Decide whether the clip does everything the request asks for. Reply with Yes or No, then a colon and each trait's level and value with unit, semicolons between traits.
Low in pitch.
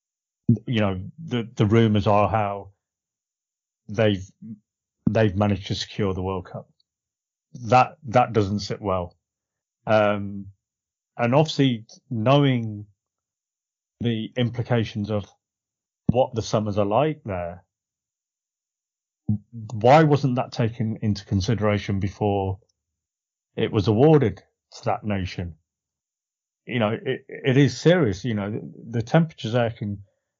Yes: low, 110 Hz